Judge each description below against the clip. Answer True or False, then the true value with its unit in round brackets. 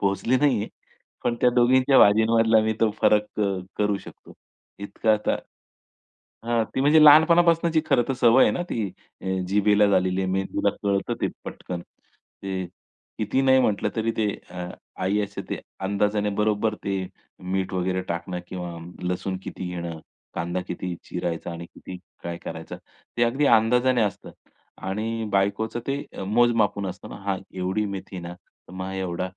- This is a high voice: False (105 Hz)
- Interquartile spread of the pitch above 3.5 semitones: True (4.0 semitones)